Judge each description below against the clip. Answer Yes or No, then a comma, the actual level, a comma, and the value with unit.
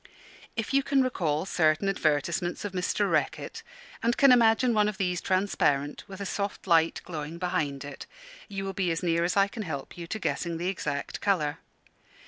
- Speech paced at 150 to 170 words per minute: No, average, 185 wpm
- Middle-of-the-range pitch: Yes, medium, 180 Hz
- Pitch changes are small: No, average, 3.9 semitones